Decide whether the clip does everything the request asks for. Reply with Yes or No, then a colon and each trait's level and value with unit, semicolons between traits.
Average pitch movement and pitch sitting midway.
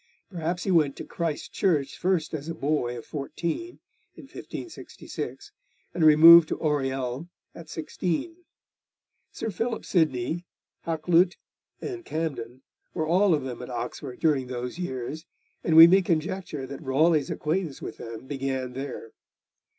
Yes: average, 4.5 semitones; medium, 155 Hz